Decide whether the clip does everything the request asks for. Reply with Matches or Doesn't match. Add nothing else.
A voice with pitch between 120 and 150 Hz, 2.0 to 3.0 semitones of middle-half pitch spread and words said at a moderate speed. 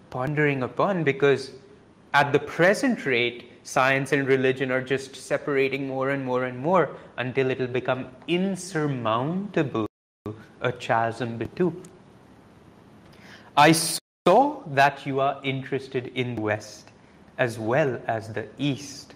Doesn't match